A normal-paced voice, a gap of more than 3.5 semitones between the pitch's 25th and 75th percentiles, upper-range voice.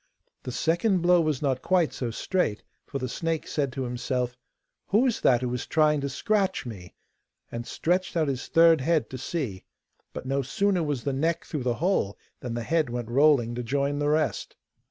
No: average, 195 wpm; average, 5.0 semitones; medium, 140 Hz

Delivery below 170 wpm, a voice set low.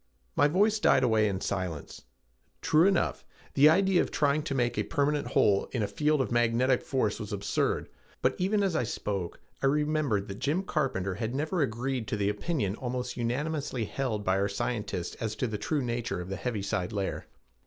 No: average, 190 wpm; low, 125 Hz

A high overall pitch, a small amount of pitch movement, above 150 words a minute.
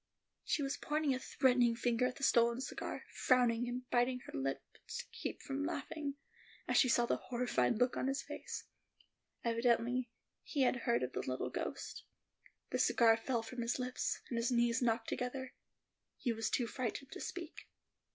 Yes: high, 245 Hz; narrow, 2.0 semitones; average, 175 wpm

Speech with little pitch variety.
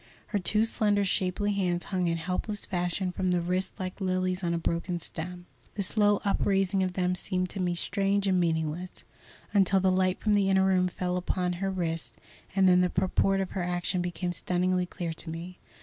Yes: narrow, 1.5 semitones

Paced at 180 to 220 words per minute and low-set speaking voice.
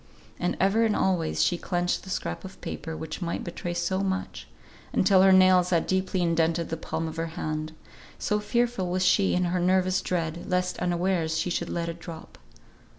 No: average, 190 wpm; medium, 180 Hz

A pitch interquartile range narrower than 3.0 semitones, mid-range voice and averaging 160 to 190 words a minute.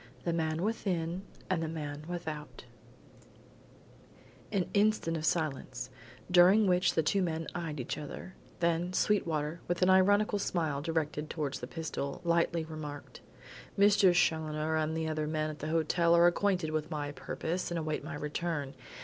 No: narrow, 2.5 semitones; medium, 165 Hz; average, 150 wpm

